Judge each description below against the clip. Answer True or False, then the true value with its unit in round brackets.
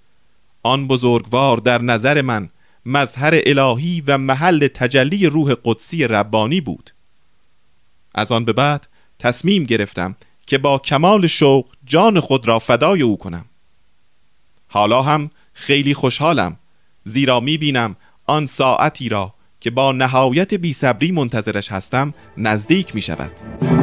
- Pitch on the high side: False (125 Hz)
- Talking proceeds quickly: False (125 wpm)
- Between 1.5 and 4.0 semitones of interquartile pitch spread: False (5.3 semitones)